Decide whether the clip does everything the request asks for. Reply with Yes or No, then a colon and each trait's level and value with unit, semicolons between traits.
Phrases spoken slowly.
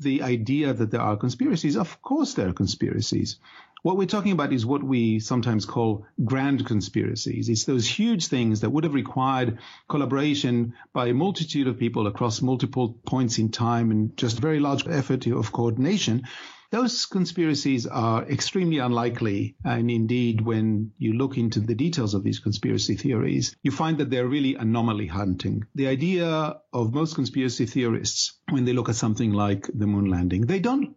No: average, 170 wpm